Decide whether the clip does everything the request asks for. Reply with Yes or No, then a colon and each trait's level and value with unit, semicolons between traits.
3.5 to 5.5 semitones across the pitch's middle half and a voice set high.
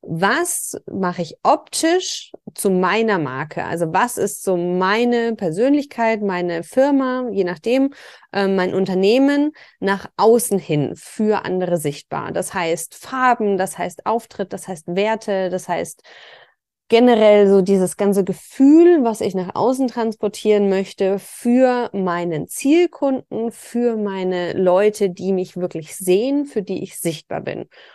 Yes: average, 4.6 semitones; high, 200 Hz